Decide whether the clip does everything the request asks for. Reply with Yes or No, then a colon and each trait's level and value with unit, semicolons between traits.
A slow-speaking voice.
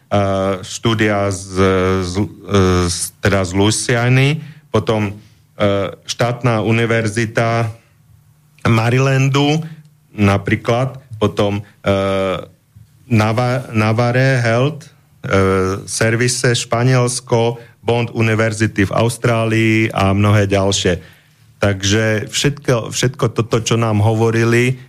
Yes: slow, 85 wpm